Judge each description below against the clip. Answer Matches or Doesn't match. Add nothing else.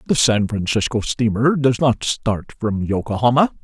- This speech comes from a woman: Doesn't match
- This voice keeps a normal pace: Matches